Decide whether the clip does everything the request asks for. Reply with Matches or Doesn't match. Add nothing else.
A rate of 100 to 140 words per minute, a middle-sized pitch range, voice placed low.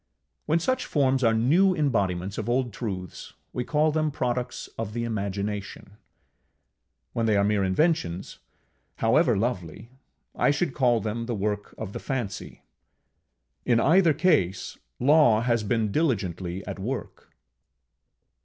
Doesn't match